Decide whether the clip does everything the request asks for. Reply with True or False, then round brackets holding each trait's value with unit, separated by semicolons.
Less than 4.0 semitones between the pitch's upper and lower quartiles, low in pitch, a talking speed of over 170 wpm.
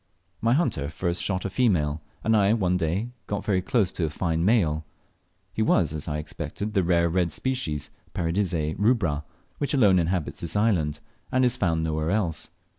False (4.7 semitones; 90 Hz; 180 wpm)